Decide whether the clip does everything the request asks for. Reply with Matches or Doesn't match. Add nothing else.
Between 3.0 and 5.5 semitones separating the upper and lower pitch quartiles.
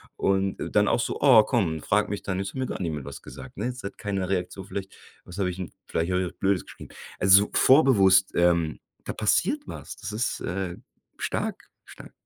Doesn't match